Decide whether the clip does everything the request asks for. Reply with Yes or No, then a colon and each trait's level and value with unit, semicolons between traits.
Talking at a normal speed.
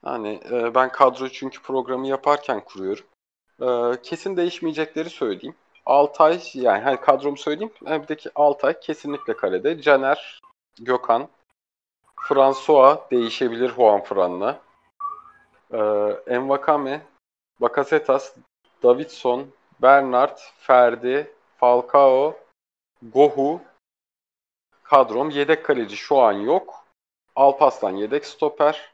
No: slow, 90 wpm